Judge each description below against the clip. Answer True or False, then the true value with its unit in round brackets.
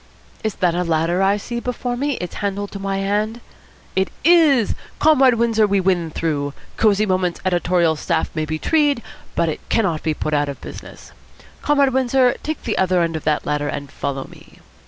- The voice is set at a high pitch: True (195 Hz)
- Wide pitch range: True (6.4 semitones)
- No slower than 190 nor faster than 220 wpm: True (195 wpm)